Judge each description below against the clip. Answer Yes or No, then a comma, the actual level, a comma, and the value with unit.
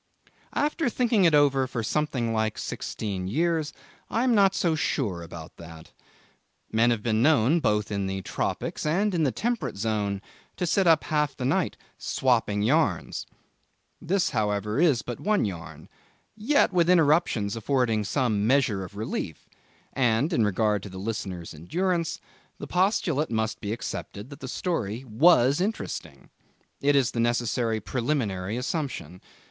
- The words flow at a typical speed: Yes, average, 150 wpm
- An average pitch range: No, wide, 7.4 semitones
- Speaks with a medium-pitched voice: No, low, 120 Hz